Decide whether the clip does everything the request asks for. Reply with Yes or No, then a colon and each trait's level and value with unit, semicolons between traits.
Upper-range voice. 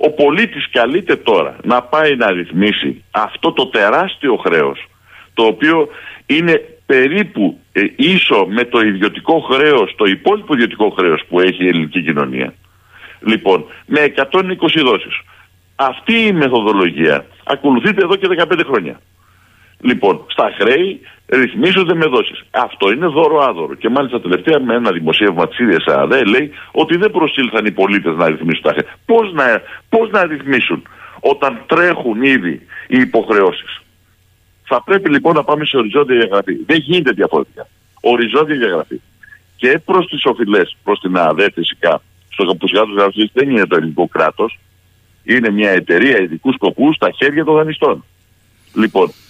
No: low, 135 Hz